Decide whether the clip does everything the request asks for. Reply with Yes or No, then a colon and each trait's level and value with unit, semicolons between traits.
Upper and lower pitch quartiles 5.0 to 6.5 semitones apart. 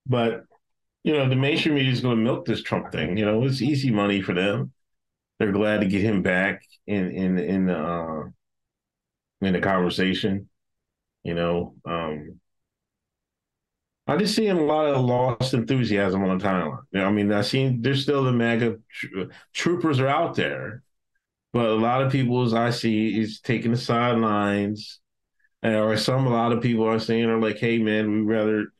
No: average, 4.3 semitones